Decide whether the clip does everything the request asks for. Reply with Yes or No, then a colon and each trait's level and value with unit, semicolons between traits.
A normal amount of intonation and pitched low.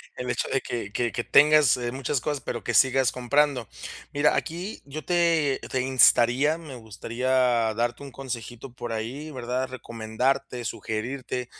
Yes: average, 3.0 semitones; low, 130 Hz